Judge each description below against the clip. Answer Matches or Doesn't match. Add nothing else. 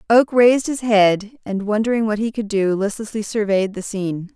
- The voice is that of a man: Doesn't match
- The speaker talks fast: Doesn't match